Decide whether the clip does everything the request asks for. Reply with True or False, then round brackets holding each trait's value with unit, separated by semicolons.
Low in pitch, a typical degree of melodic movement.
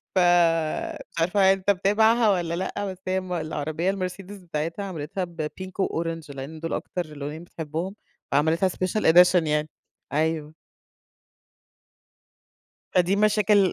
False (175 Hz; 3.2 semitones)